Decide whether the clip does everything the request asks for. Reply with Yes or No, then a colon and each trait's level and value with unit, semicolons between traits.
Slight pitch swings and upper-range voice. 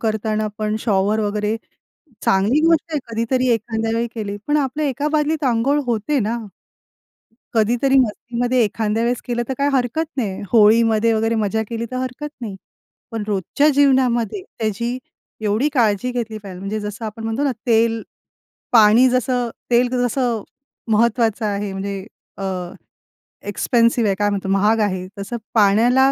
No: average, 3.0 semitones; high, 225 Hz